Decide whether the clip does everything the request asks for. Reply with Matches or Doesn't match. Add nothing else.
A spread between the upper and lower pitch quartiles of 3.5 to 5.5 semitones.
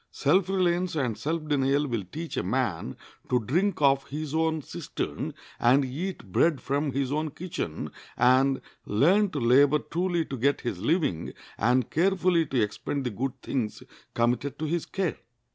Matches